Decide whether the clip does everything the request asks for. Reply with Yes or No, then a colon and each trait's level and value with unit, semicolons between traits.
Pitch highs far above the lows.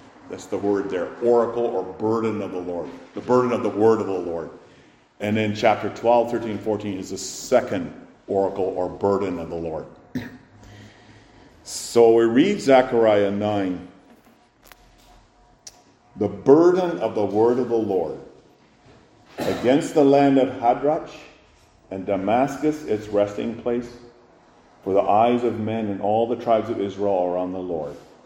No: average, 3.6 semitones